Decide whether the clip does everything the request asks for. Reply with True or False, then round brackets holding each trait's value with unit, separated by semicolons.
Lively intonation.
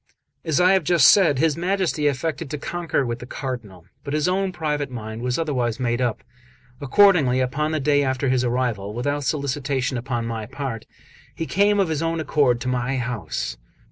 False (4.3 semitones)